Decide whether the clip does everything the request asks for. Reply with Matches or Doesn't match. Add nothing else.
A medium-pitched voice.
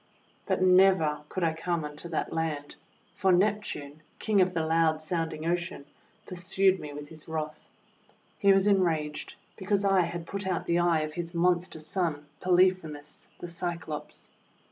Matches